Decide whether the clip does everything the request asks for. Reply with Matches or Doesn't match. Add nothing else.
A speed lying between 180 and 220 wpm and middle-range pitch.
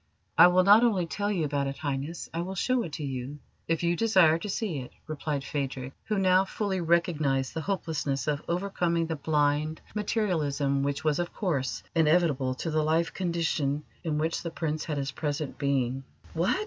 Matches